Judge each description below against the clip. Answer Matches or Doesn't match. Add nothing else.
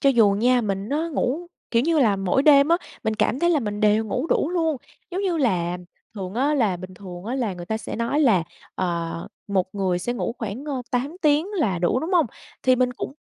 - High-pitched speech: Matches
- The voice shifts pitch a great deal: Matches